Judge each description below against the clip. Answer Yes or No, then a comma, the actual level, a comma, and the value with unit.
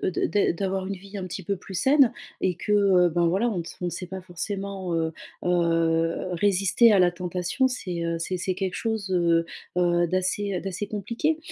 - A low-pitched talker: No, medium, 185 Hz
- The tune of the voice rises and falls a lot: No, narrow, 2.5 semitones